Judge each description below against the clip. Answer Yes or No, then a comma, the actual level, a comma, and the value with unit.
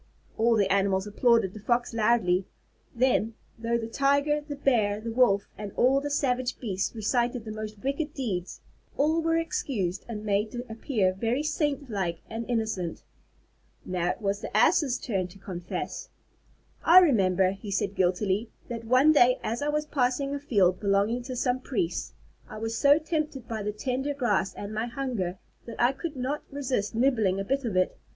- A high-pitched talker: Yes, high, 230 Hz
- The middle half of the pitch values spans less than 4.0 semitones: No, average, 5.2 semitones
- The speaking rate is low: No, average, 180 wpm